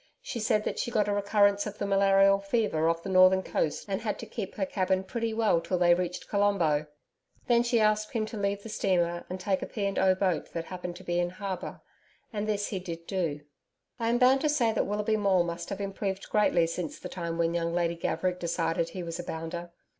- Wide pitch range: No, average, 3.3 semitones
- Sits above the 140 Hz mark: Yes, high, 190 Hz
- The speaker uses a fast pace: Yes, fast, 230 wpm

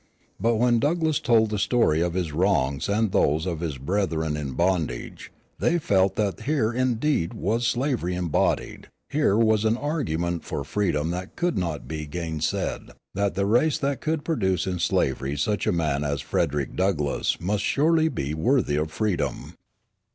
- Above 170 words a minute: No, average, 165 wpm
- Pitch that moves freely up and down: Yes, wide, 6.9 semitones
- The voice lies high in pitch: No, very low, 95 Hz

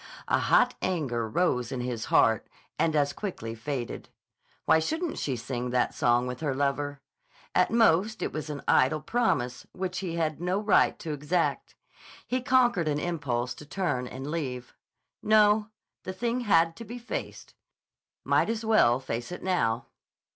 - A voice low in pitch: No, medium, 155 Hz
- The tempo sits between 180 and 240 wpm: No, average, 165 wpm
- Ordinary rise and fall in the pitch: No, wide, 7.3 semitones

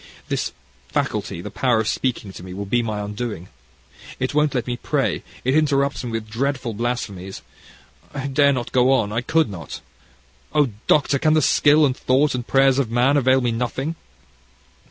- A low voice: Yes, low, 125 Hz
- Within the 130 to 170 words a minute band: No, average, 180 wpm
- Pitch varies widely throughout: No, average, 3.7 semitones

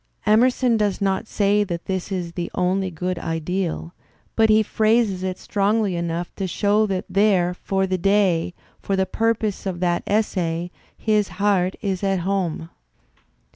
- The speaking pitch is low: No, high, 190 Hz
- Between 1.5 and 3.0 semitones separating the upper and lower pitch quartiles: Yes, average, 2.7 semitones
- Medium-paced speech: Yes, average, 160 wpm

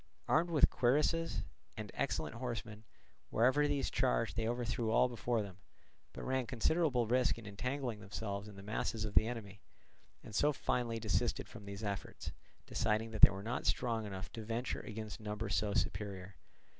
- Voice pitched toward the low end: Yes, low, 115 Hz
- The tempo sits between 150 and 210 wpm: Yes, average, 170 wpm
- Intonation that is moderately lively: Yes, average, 3.1 semitones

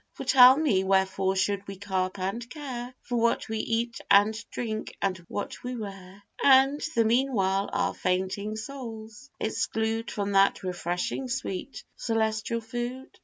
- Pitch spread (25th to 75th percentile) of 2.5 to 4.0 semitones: Yes, average, 3.7 semitones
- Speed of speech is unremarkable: Yes, average, 145 wpm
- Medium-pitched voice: No, high, 220 Hz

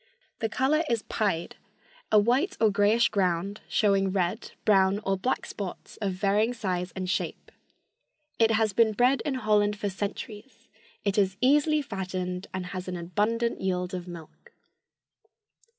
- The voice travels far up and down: No, average, 3.5 semitones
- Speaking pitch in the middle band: No, high, 205 Hz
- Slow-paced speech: No, average, 150 wpm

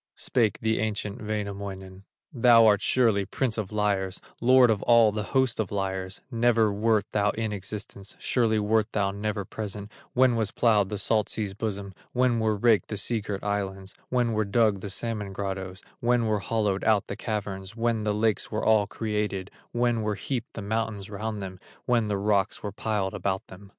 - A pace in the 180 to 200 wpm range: Yes, average, 185 wpm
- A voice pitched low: Yes, low, 105 Hz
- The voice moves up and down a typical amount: No, narrow, 2.1 semitones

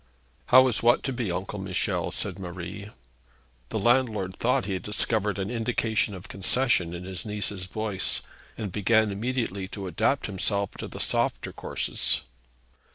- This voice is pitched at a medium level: No, low, 105 Hz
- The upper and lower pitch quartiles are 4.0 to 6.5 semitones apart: No, average, 3.4 semitones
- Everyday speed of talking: Yes, average, 155 wpm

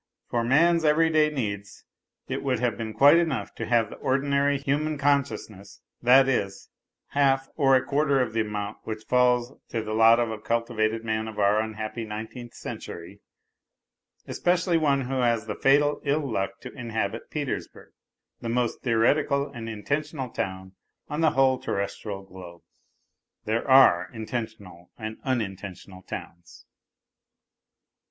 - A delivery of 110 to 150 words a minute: Yes, average, 145 wpm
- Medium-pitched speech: No, low, 120 Hz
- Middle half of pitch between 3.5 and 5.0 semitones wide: Yes, average, 4.4 semitones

